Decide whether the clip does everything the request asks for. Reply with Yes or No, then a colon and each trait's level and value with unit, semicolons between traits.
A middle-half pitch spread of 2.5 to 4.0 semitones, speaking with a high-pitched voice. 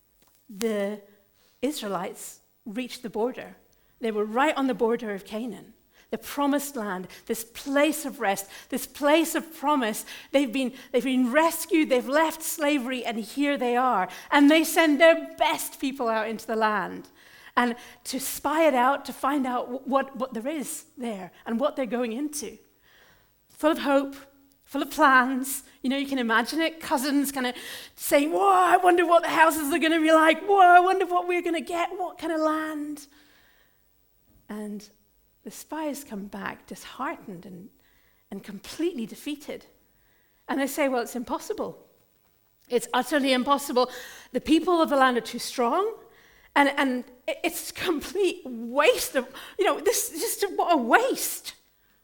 No: average, 4.6 semitones; very high, 275 Hz